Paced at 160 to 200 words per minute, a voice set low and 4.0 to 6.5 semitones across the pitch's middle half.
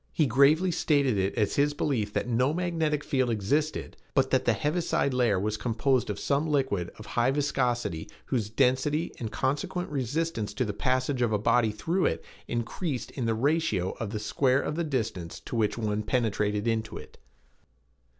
Yes: average, 180 wpm; low, 125 Hz; average, 5.3 semitones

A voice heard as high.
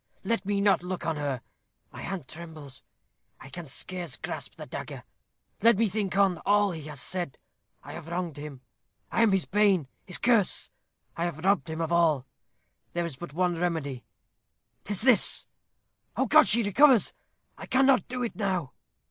No: medium, 180 Hz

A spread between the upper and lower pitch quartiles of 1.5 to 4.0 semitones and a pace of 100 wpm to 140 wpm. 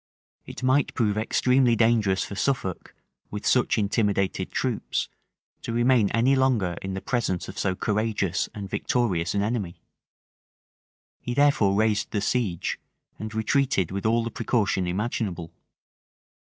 Yes: average, 3.7 semitones; slow, 135 wpm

